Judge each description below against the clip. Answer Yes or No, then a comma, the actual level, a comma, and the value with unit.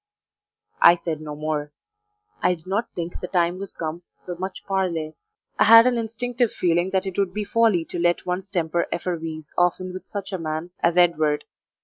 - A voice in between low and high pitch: Yes, medium, 175 Hz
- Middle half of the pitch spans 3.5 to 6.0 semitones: No, average, 2.8 semitones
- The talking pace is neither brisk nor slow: Yes, average, 190 wpm